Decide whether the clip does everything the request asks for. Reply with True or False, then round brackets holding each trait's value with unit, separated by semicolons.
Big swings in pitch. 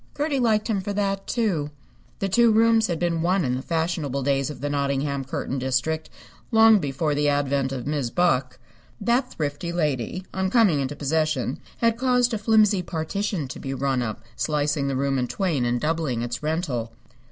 True (6.4 semitones)